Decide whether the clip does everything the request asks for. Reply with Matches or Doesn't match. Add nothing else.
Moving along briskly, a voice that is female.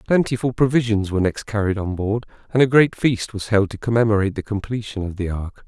Doesn't match